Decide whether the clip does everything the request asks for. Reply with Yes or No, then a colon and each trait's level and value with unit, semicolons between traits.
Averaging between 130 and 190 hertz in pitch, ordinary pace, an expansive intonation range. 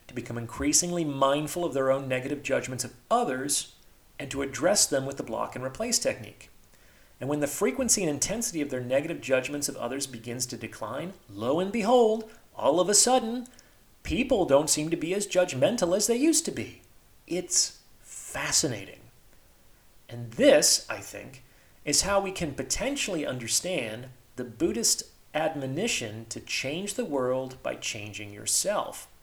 Yes: medium, 140 Hz; average, 160 wpm; wide, 6.8 semitones